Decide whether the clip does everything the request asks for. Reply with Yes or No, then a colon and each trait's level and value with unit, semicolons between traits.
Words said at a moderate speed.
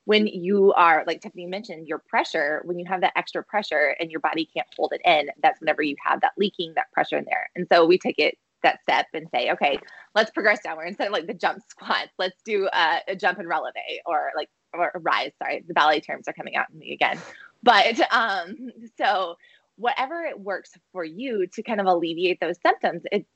No: fast, 225 wpm